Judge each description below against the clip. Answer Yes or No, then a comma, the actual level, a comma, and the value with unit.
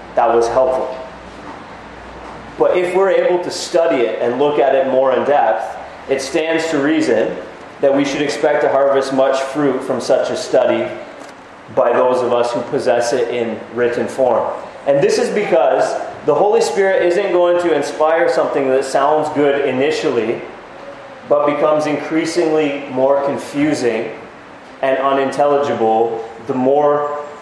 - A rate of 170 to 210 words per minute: No, average, 150 wpm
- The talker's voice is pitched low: No, medium, 145 Hz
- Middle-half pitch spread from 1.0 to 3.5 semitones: Yes, average, 2.8 semitones